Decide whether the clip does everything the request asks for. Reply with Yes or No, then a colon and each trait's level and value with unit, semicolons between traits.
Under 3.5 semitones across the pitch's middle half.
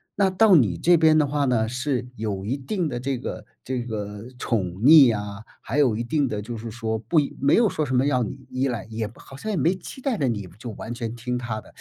No: average, 4.8 semitones